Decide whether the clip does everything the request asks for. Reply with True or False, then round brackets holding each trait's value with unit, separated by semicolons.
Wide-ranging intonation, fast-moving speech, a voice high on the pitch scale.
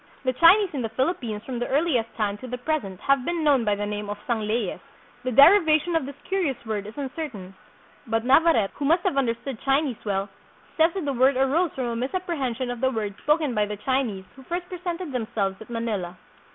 True (5.9 semitones; 215 wpm; 255 Hz)